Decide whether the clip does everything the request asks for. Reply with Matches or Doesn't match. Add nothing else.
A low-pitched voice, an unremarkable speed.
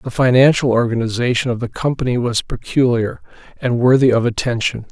Matches